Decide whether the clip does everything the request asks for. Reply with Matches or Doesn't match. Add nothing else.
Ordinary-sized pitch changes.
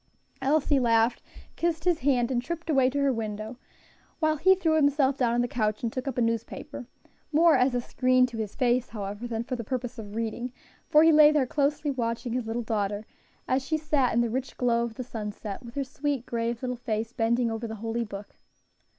Matches